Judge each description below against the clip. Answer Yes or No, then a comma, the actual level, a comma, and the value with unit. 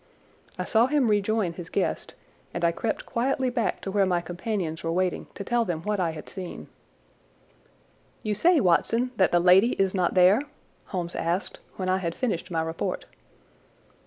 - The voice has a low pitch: No, high, 190 Hz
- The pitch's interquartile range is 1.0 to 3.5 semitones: No, average, 4.4 semitones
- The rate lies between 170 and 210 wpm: Yes, average, 175 wpm